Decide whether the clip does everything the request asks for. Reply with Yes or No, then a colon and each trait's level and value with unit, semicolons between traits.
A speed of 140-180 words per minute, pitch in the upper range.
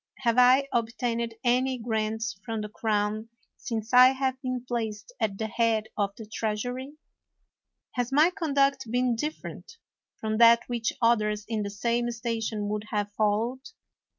Yes: average, 150 wpm; high, 230 Hz